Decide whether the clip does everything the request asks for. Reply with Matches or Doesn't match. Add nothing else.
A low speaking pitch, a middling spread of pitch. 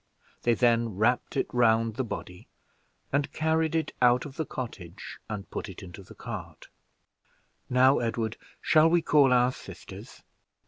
Matches